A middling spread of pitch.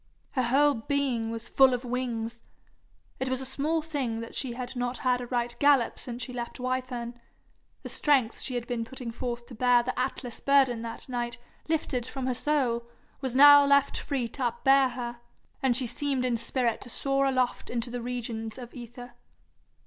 No: narrow, 2.0 semitones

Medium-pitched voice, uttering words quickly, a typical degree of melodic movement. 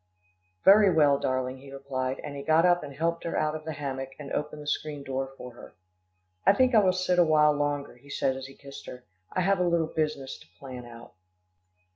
Yes: medium, 145 Hz; fast, 225 wpm; average, 3.6 semitones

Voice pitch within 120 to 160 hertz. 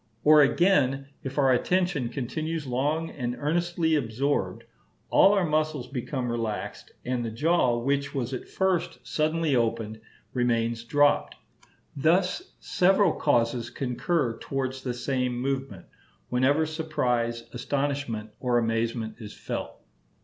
Yes: low, 135 Hz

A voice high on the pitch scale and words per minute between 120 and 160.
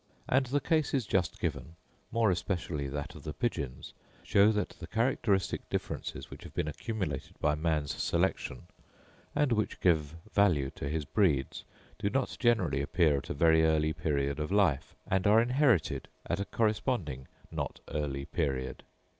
No: very low, 85 Hz; average, 155 wpm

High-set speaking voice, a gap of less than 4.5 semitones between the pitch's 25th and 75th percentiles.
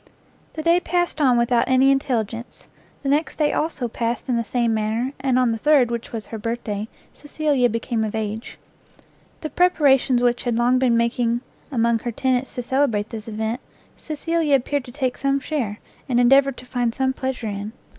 Yes: high, 245 Hz; average, 3.0 semitones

